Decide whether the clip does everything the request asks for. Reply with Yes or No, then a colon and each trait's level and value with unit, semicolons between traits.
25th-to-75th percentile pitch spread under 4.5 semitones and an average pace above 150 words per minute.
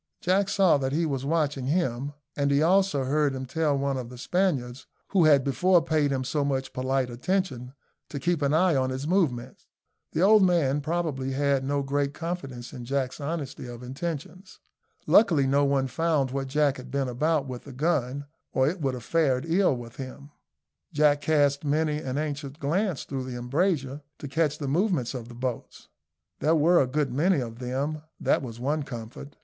Yes: average, 3.5 semitones; average, 190 wpm